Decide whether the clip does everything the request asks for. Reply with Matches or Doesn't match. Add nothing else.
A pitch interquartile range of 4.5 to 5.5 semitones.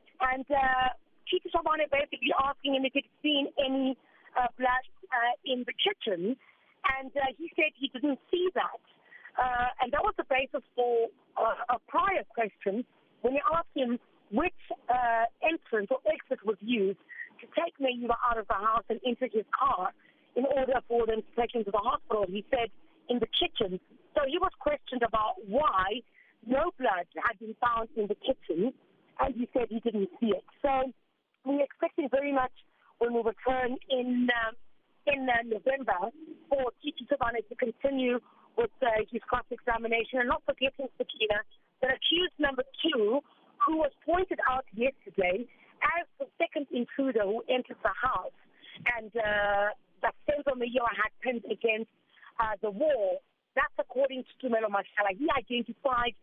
Doesn't match